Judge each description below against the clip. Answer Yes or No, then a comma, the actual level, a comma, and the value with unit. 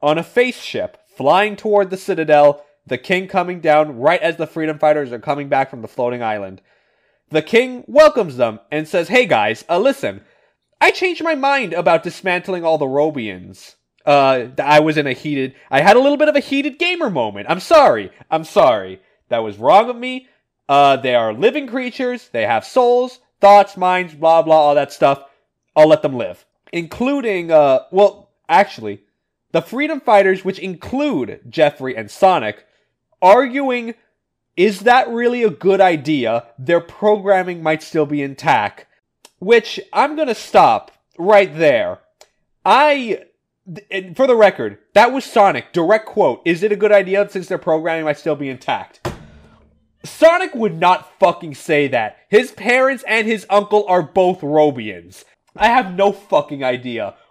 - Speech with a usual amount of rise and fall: No, wide, 7.9 semitones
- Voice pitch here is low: No, medium, 180 Hz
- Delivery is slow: No, average, 165 wpm